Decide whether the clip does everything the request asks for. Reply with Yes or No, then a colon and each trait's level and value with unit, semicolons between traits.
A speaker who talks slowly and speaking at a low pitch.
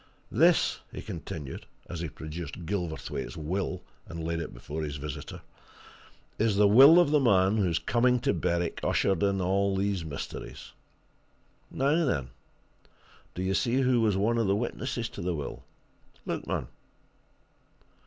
No: average, 150 wpm; very low, 95 Hz